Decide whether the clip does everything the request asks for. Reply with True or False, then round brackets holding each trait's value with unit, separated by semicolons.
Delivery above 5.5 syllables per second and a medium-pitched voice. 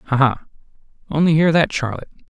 True (6.2 syllables/s; 145 Hz)